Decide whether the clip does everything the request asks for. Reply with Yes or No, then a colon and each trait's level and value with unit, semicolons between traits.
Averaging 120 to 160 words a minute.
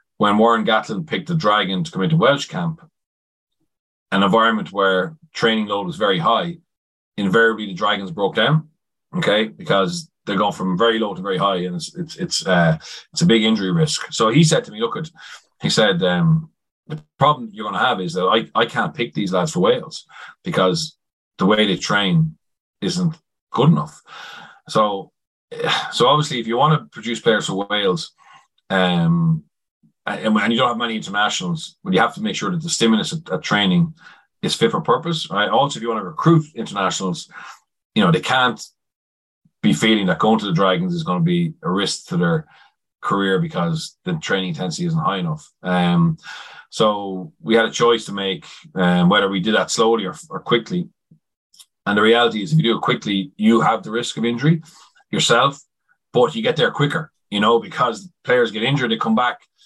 No: average, 195 wpm